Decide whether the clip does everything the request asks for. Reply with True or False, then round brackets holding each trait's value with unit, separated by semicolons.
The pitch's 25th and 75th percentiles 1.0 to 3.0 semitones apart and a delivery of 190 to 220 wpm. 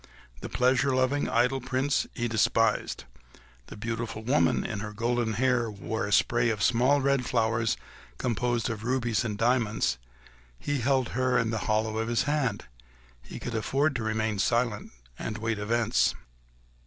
False (2.5 semitones; 160 wpm)